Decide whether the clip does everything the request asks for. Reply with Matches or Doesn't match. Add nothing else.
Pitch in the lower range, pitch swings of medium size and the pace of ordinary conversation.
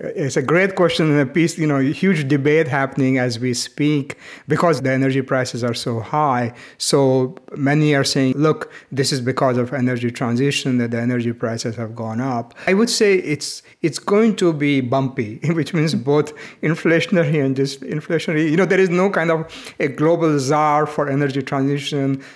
Doesn't match